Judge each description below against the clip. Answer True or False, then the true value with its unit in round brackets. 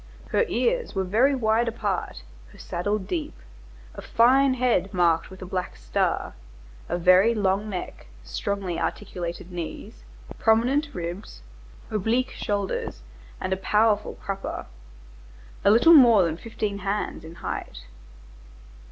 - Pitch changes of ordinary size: True (4.3 semitones)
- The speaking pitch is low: False (200 Hz)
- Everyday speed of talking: False (125 wpm)